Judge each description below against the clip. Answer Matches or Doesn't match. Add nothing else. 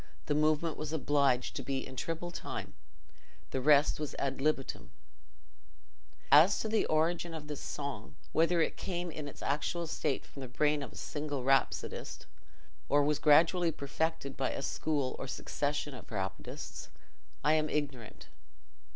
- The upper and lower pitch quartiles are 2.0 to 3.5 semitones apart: Matches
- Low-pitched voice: Doesn't match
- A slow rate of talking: Doesn't match